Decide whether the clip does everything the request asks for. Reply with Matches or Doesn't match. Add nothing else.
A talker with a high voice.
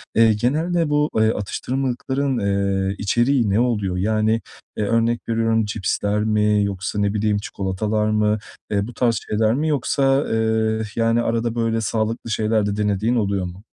Doesn't match